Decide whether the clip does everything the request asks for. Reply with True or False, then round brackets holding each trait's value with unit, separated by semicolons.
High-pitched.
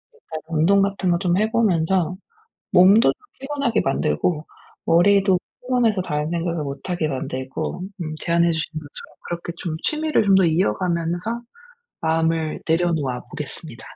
False (170 Hz)